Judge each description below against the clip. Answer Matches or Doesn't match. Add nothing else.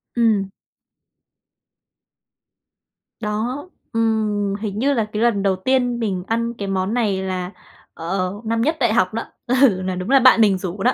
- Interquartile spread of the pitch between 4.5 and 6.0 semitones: Doesn't match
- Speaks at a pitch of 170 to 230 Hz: Matches